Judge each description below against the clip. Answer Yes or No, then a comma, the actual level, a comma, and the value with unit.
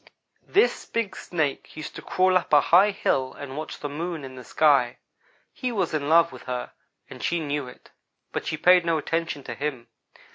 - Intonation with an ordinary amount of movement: Yes, average, 3.9 semitones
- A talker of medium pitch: Yes, medium, 155 Hz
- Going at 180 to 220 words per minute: Yes, average, 195 wpm